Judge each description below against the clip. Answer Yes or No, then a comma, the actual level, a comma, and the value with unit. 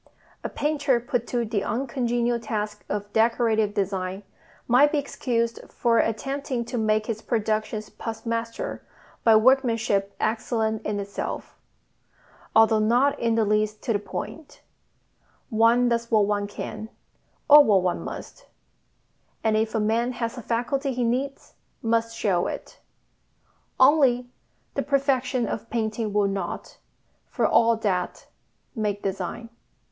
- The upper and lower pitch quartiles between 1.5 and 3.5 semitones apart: Yes, narrow, 2.5 semitones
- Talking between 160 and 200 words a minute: No, slow, 135 wpm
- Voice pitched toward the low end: No, high, 230 Hz